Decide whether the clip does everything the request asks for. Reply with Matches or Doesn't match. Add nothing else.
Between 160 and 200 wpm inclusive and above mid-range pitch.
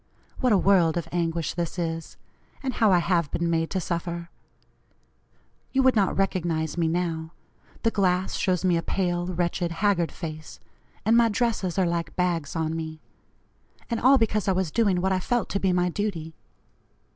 Doesn't match